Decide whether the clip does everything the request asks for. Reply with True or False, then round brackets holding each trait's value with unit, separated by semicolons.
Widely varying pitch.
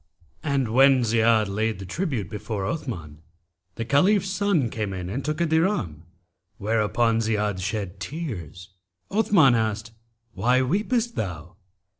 True (7.1 semitones)